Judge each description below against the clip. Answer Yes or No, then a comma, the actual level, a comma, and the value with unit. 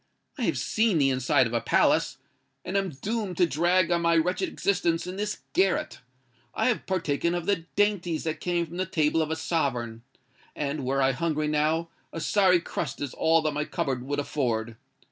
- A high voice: No, medium, 165 Hz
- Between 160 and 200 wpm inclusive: Yes, average, 185 wpm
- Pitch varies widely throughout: No, average, 4.3 semitones